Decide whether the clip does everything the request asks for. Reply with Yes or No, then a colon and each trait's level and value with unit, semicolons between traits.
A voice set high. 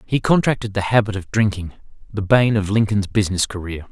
No: low, 105 Hz